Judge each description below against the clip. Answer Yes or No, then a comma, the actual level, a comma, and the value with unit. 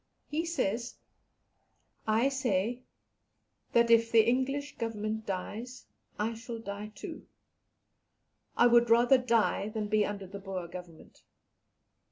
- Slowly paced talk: Yes, slow, 120 wpm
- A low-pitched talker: No, high, 225 Hz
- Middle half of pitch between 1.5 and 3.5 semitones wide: Yes, average, 2.8 semitones